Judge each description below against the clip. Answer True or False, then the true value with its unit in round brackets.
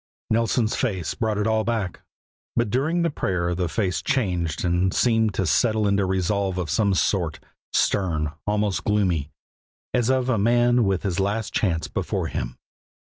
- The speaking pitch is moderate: False (100 Hz)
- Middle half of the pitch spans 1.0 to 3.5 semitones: False (3.9 semitones)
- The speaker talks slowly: False (160 wpm)